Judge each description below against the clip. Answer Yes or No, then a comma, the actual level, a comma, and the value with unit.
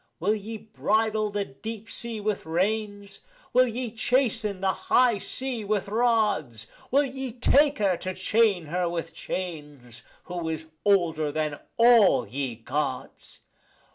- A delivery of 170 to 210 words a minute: No, average, 140 wpm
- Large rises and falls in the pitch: Yes, wide, 5.7 semitones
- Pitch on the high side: Yes, high, 205 Hz